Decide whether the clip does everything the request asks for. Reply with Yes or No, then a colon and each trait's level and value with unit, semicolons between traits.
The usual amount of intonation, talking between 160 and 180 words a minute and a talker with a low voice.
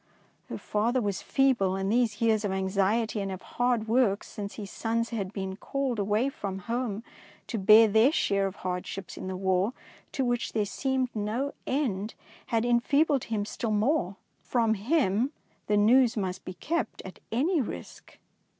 No: average, 3.7 semitones; average, 170 wpm; high, 220 Hz